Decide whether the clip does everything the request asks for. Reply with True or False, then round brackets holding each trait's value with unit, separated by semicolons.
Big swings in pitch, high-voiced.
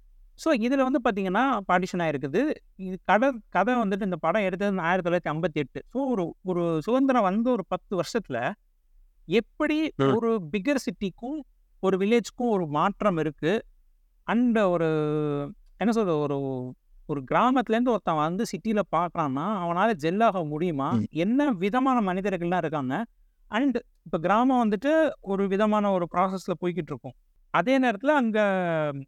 True (6.0 semitones; 195 Hz)